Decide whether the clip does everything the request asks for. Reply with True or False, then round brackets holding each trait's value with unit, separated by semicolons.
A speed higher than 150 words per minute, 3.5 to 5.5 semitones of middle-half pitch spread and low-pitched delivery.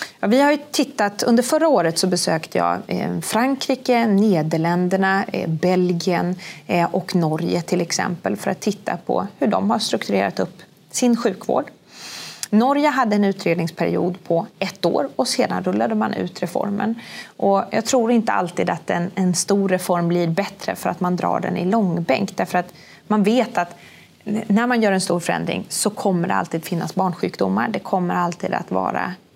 False (170 wpm; 3.9 semitones; 190 Hz)